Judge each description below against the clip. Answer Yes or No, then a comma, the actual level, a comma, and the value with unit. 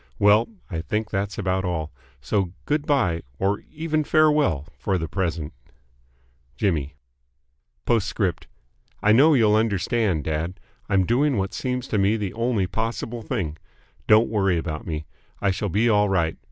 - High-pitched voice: No, low, 100 Hz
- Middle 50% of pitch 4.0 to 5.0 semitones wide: Yes, average, 4.6 semitones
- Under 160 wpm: Yes, average, 150 wpm